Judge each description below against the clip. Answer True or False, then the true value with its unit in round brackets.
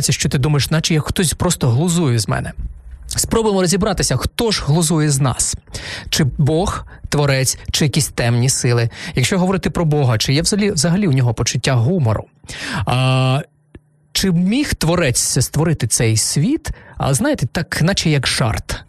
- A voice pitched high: False (140 Hz)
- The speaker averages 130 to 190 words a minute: True (155 wpm)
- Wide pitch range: True (5.8 semitones)